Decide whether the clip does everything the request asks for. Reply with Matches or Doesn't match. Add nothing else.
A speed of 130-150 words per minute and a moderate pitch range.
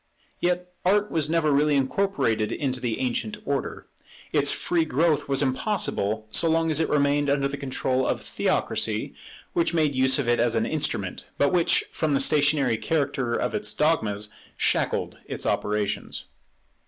Doesn't match